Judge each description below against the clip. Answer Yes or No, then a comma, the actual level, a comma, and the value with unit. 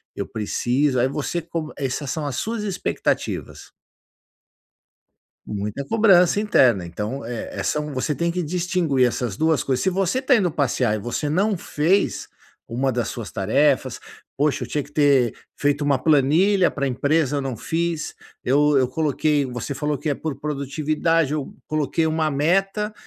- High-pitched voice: No, medium, 145 Hz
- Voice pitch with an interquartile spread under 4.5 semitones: Yes, average, 4.0 semitones